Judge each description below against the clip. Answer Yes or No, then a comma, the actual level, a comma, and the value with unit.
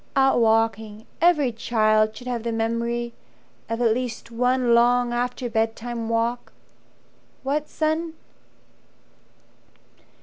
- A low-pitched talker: No, high, 235 Hz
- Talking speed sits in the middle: No, slow, 105 wpm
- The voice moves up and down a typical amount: No, narrow, 1.7 semitones